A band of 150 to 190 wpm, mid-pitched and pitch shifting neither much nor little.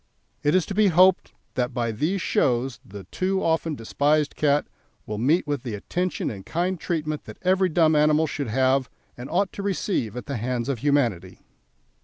No: average, 185 wpm; medium, 145 Hz; wide, 6.0 semitones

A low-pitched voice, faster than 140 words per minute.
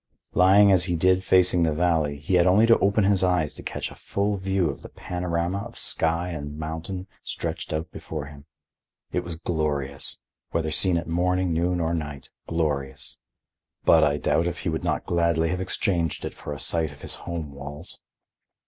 Yes: very low, 85 Hz; average, 190 wpm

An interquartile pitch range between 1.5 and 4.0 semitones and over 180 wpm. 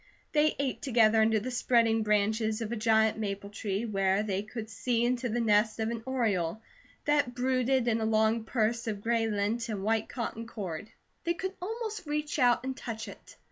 Yes: narrow, 2.4 semitones; average, 190 wpm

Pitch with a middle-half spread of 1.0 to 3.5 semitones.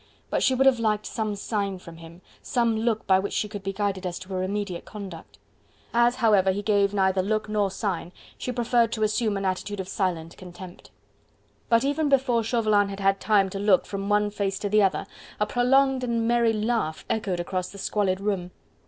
Yes: average, 3.0 semitones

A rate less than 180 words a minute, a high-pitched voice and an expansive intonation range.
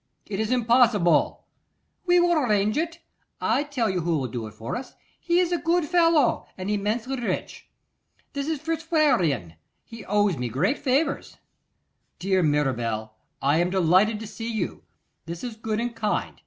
Yes: average, 165 wpm; high, 220 Hz; wide, 8.5 semitones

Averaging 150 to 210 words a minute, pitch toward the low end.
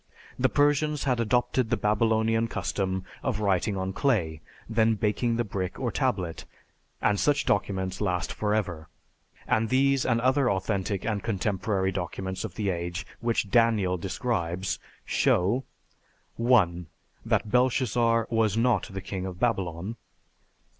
No: slow, 135 wpm; low, 105 Hz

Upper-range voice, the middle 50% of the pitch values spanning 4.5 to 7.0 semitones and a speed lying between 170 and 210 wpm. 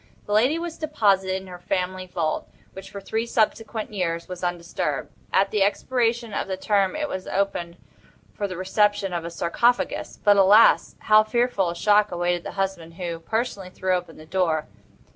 No: high, 195 Hz; average, 3.3 semitones; average, 180 wpm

